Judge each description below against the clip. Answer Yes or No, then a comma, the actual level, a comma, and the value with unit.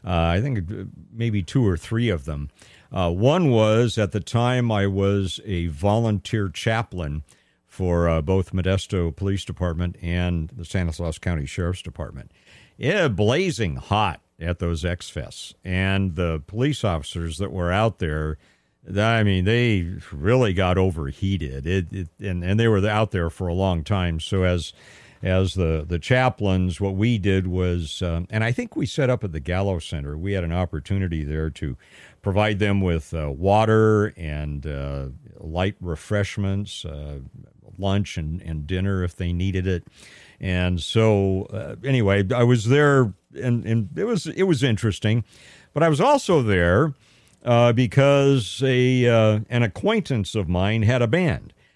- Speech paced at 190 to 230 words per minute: No, average, 160 wpm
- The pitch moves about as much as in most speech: Yes, average, 4.5 semitones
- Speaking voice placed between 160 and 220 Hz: No, very low, 95 Hz